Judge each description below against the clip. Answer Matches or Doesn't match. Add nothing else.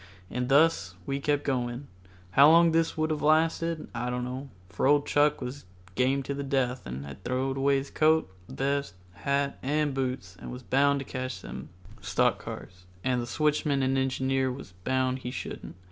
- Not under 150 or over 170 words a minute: Doesn't match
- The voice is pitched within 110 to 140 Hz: Matches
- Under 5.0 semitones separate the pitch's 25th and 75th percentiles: Matches